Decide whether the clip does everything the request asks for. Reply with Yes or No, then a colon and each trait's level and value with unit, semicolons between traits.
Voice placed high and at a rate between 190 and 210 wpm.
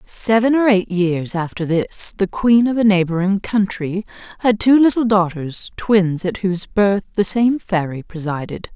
No: high, 200 Hz; average, 165 wpm